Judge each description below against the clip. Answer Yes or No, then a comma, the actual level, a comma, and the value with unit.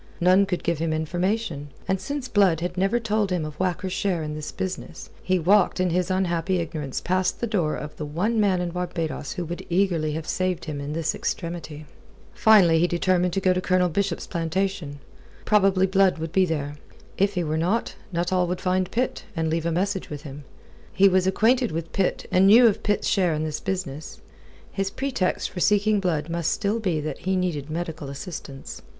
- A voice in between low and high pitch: Yes, medium, 180 Hz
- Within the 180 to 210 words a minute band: Yes, average, 200 wpm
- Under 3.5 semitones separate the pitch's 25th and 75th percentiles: Yes, average, 3.1 semitones